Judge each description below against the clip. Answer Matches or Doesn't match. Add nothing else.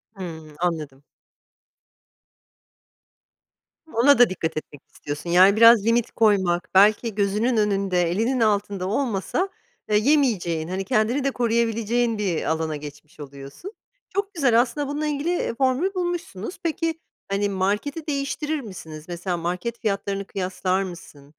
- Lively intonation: Matches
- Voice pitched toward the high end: Matches